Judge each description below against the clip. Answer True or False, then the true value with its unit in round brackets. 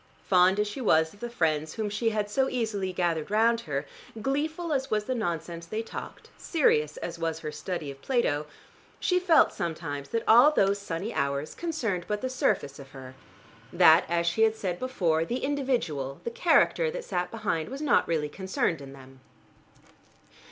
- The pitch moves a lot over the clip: True (6.9 semitones)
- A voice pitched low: False (190 Hz)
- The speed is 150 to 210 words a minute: True (180 wpm)